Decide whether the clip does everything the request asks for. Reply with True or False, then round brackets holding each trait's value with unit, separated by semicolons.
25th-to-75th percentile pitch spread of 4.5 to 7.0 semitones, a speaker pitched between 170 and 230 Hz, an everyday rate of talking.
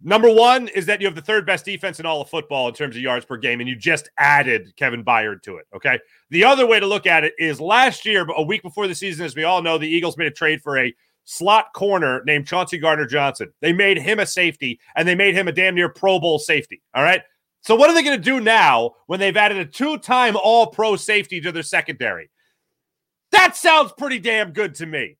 False (5.2 semitones; 185 Hz; 250 wpm)